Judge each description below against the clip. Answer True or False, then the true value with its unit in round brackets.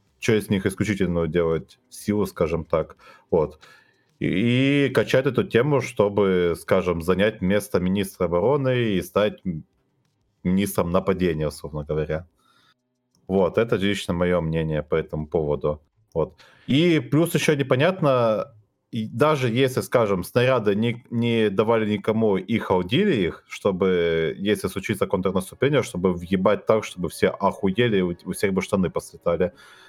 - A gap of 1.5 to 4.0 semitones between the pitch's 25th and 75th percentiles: False (5.1 semitones)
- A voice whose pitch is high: False (100 Hz)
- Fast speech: False (130 wpm)